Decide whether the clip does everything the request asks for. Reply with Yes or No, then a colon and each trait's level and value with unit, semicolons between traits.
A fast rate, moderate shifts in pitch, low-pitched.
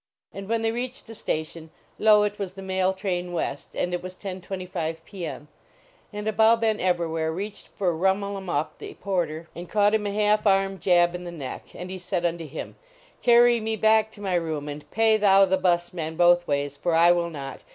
No: fast, 215 wpm; average, 3.4 semitones; medium, 185 Hz